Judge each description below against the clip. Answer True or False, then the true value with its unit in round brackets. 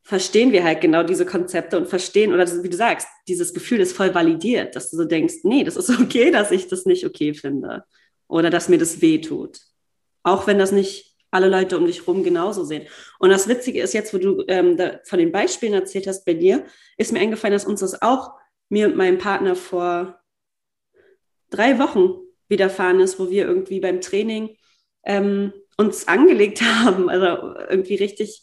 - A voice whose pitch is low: False (200 Hz)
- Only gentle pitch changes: False (5.2 semitones)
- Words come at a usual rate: False (195 wpm)